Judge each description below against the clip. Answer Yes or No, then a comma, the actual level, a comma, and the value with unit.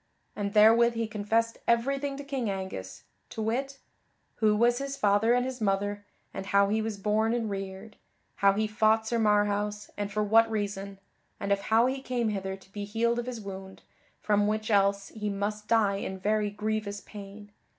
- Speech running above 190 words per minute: No, average, 185 wpm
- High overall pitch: Yes, high, 210 Hz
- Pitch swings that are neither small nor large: No, narrow, 2.1 semitones